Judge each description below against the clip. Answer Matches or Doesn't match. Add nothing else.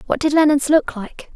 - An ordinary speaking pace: Doesn't match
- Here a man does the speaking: Doesn't match